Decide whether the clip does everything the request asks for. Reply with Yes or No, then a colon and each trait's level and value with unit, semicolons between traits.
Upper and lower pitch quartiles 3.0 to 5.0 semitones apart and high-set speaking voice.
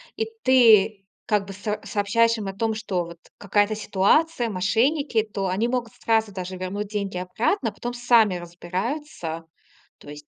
Yes: average, 3.7 semitones; high, 210 Hz